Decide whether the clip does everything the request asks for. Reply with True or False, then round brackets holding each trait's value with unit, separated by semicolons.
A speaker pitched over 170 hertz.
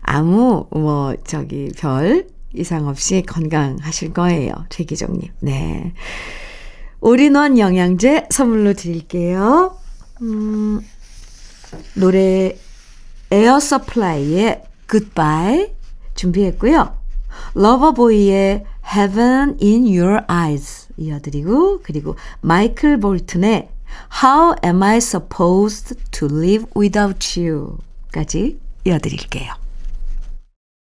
True (190 Hz)